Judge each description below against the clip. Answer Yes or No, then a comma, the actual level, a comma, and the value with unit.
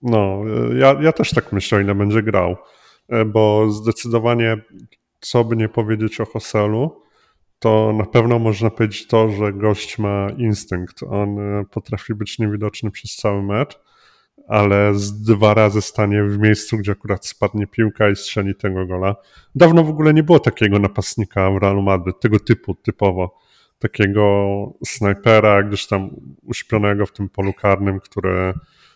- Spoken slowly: No, average, 150 wpm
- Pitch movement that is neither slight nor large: No, narrow, 2.0 semitones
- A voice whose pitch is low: Yes, low, 105 Hz